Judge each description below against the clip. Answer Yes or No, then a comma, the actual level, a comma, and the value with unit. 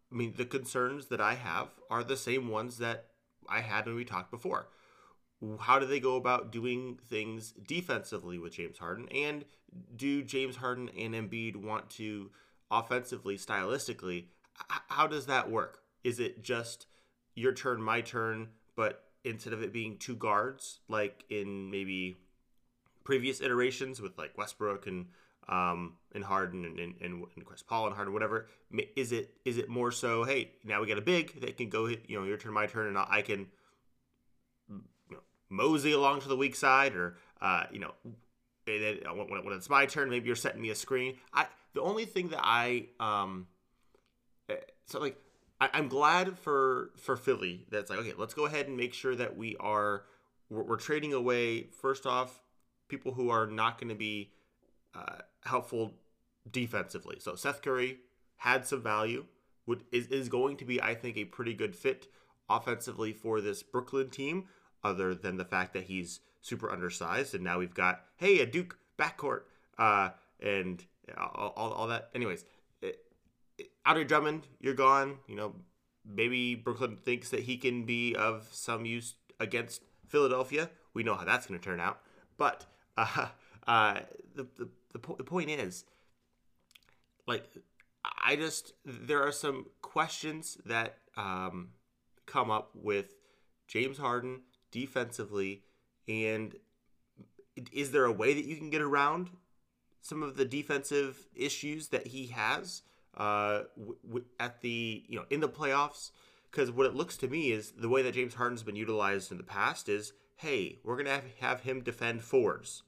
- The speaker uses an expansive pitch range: No, average, 4.1 semitones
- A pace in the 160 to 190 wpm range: Yes, average, 170 wpm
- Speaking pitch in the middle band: No, low, 120 Hz